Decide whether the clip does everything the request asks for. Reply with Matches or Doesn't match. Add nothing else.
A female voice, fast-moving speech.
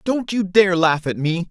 Doesn't match